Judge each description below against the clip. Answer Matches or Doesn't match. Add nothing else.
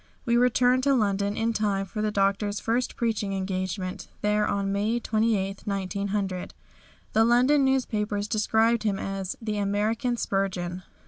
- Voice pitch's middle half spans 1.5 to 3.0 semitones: Matches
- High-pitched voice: Matches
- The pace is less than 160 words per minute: Matches